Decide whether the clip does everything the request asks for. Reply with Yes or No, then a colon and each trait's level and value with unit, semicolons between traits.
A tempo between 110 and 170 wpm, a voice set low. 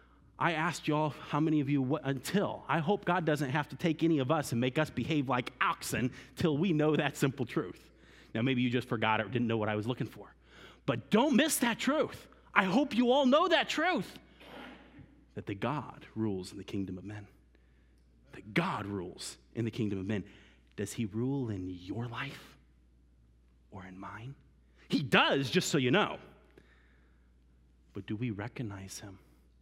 No: average, 190 wpm; low, 120 Hz